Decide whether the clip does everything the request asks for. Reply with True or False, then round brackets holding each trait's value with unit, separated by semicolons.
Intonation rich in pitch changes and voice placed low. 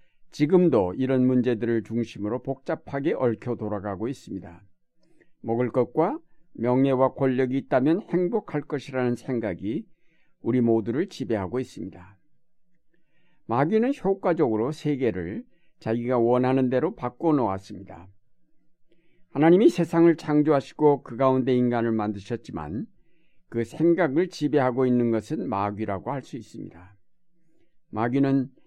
True (6.0 semitones; 130 Hz)